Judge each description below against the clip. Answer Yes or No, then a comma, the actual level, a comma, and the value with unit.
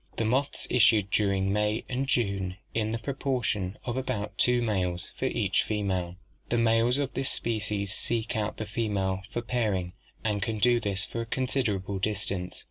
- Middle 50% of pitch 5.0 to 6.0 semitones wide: No, average, 3.4 semitones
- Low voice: Yes, low, 110 Hz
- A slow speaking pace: No, average, 170 wpm